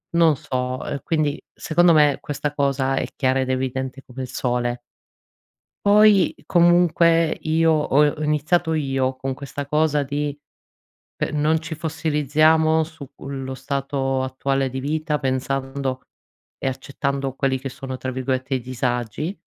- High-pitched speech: No, medium, 140 Hz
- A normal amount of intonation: Yes, average, 3.0 semitones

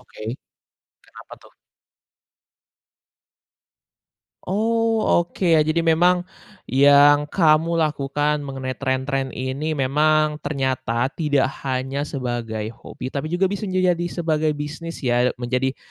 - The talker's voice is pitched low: No, medium, 145 Hz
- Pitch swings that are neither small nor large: Yes, average, 4.0 semitones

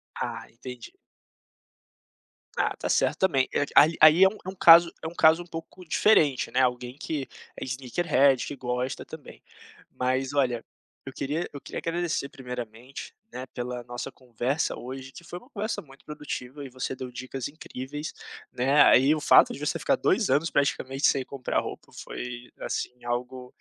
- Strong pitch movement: No, average, 3.6 semitones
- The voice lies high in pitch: No, low, 135 Hz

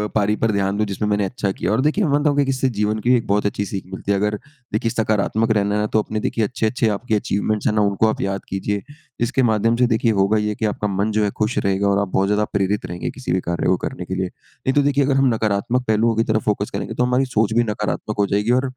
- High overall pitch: No, low, 105 Hz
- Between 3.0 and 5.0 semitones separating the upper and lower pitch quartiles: No, narrow, 2.4 semitones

